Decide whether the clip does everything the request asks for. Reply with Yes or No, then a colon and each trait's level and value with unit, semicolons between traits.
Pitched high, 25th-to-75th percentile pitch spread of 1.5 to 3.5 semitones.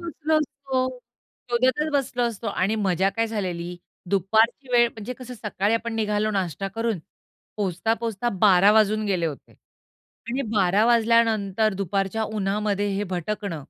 Yes: high, 215 Hz; average, 3.1 semitones